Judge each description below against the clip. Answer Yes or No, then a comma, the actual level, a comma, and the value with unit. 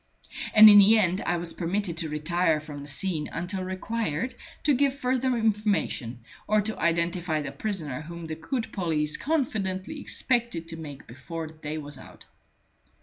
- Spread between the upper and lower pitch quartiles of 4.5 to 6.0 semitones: Yes, wide, 5.5 semitones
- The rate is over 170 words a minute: No, average, 165 wpm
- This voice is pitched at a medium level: Yes, medium, 175 Hz